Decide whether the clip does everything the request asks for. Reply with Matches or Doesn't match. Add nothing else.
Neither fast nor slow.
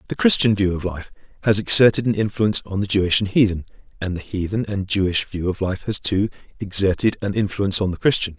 Doesn't match